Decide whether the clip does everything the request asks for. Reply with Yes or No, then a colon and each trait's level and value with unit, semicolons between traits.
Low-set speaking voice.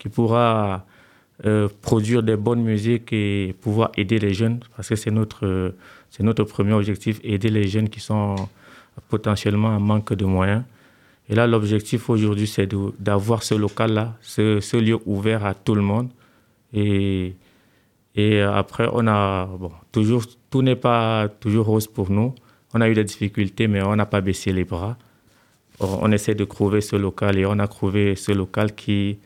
Yes: low, 105 Hz